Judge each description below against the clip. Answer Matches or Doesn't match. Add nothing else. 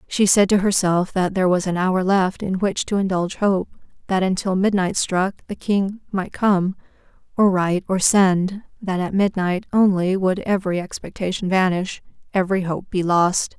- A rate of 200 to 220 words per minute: Doesn't match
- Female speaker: Matches